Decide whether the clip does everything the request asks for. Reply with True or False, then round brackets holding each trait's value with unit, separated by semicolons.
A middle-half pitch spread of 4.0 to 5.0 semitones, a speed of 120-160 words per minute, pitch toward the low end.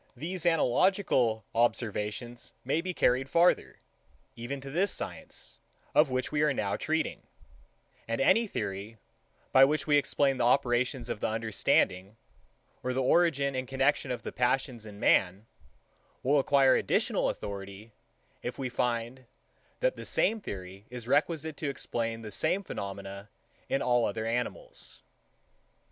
True (4.5 semitones; 140 wpm; 125 Hz)